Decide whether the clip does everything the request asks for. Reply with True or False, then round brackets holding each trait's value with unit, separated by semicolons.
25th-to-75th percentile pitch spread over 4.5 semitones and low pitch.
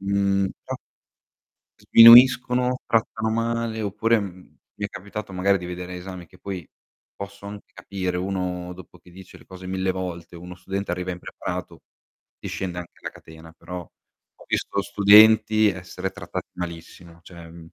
False (2.5 semitones; 95 Hz)